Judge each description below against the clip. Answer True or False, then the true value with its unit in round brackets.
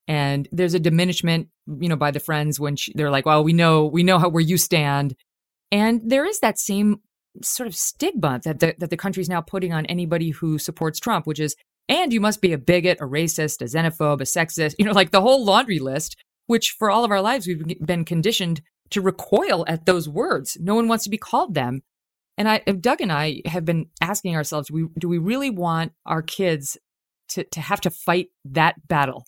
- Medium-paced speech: False (225 wpm)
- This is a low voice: False (170 Hz)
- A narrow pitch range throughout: False (4.0 semitones)